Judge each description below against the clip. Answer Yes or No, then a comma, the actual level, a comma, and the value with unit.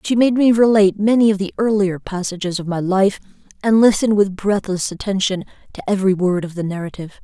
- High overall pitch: Yes, high, 200 Hz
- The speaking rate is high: No, average, 190 wpm